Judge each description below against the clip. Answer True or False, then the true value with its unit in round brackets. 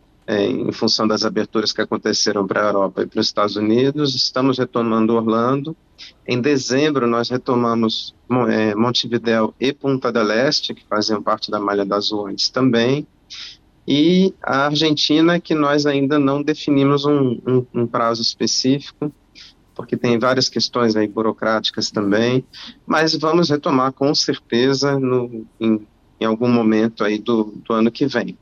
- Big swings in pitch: False (4.0 semitones)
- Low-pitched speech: True (120 Hz)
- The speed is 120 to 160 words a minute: True (150 wpm)